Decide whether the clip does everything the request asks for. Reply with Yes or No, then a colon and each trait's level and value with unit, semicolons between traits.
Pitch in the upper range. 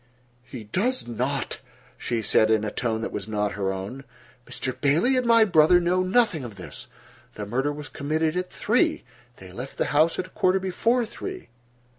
No: medium, 145 Hz